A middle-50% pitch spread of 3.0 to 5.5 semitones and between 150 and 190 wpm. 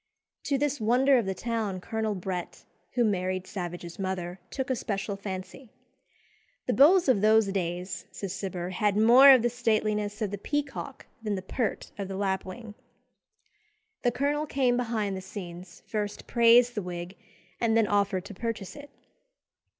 Yes: average, 4.1 semitones; average, 160 wpm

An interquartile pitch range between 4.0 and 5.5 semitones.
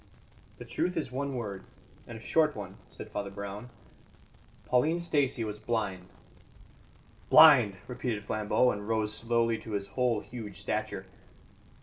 No: average, 3.6 semitones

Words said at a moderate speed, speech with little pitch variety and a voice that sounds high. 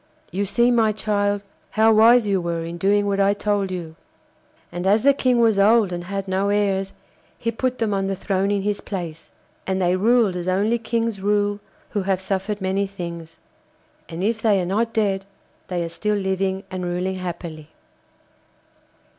Yes: average, 180 wpm; narrow, 2.3 semitones; high, 195 Hz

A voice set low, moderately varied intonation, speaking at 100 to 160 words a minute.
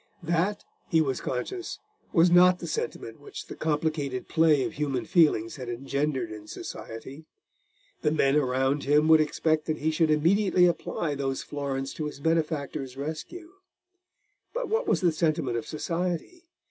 No: medium, 155 Hz; average, 3.6 semitones; average, 155 wpm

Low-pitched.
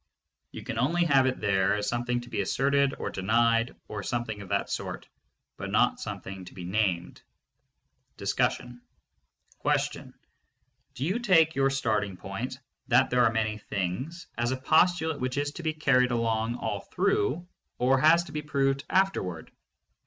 Yes: low, 125 Hz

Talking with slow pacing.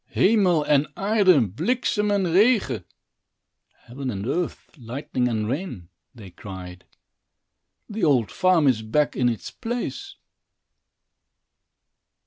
Yes: slow, 110 wpm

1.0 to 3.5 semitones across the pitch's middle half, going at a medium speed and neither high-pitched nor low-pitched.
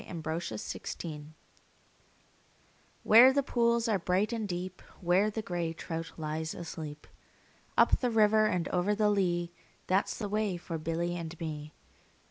No: average, 4.4 semitones; average, 150 wpm; medium, 175 Hz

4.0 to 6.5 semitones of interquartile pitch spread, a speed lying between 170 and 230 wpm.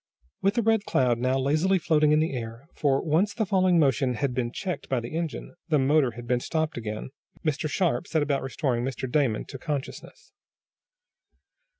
Yes: average, 4.3 semitones; average, 185 wpm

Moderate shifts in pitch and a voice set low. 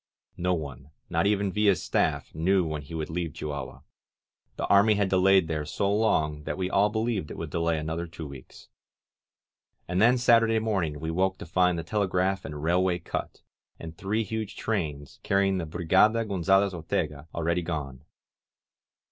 Yes: average, 3.9 semitones; very low, 90 Hz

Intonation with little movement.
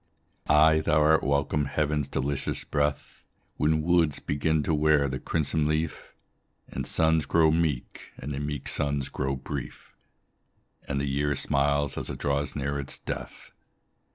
Yes: narrow, 1.6 semitones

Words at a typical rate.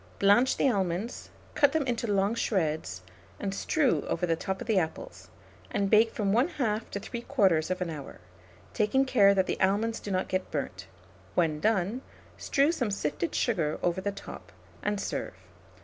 Yes: average, 165 wpm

